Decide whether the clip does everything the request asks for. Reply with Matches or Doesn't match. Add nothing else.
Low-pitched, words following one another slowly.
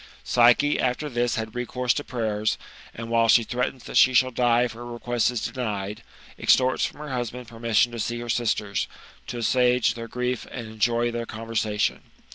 Doesn't match